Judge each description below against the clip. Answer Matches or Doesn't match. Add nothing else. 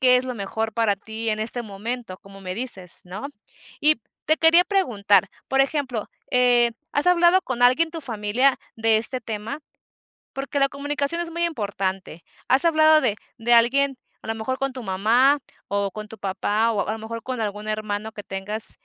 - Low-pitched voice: Doesn't match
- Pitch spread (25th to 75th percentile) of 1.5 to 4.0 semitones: Doesn't match